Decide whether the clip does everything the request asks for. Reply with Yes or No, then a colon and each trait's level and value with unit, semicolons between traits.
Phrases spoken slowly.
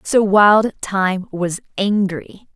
Yes: slow, 120 wpm